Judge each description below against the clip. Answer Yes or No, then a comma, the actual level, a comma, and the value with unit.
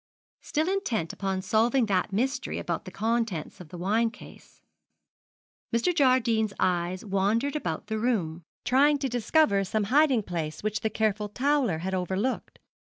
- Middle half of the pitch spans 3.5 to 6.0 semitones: Yes, average, 5.0 semitones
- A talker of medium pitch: No, high, 220 Hz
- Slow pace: No, average, 145 wpm